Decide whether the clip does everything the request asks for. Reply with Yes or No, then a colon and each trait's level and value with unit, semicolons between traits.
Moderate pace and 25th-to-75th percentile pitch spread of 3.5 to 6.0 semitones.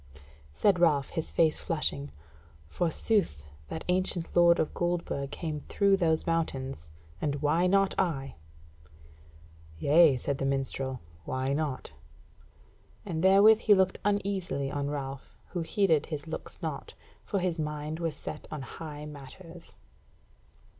No: slow, 130 wpm; average, 4.1 semitones